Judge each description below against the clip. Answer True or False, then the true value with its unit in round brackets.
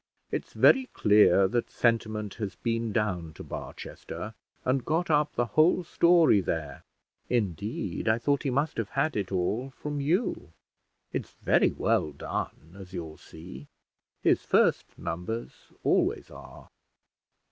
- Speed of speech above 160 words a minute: False (135 wpm)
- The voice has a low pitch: True (110 Hz)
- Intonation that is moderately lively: False (7.2 semitones)